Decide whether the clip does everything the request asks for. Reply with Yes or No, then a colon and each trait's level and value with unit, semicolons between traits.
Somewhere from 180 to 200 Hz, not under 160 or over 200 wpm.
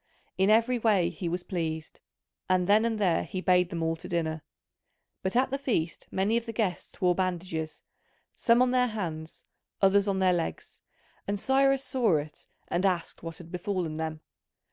Yes: medium, 185 Hz; average, 180 wpm